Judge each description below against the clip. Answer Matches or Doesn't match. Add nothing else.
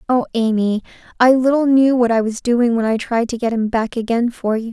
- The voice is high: Matches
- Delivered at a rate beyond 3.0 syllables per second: Matches